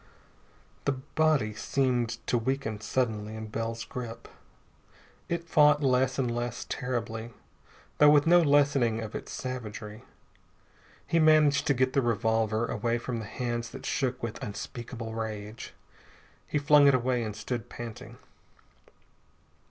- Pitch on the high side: No, low, 120 Hz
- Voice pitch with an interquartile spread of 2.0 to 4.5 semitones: Yes, average, 3.4 semitones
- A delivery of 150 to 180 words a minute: No, slow, 135 wpm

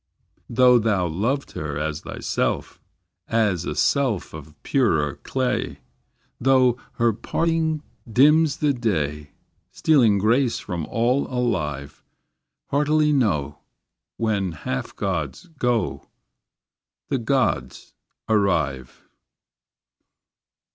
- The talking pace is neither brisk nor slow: No, slow, 95 wpm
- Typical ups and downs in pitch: No, wide, 8.9 semitones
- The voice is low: Yes, low, 115 Hz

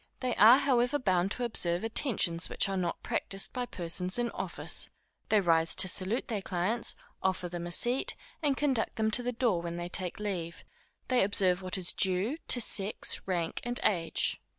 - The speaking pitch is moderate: No, high, 195 Hz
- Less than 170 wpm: No, average, 185 wpm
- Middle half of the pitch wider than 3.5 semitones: Yes, average, 5.3 semitones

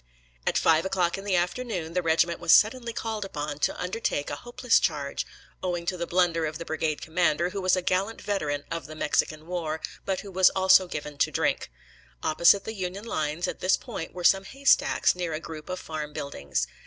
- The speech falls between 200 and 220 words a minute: Yes, fast, 205 wpm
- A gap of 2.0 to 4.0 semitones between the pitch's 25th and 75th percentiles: Yes, average, 3.5 semitones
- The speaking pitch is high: No, medium, 175 Hz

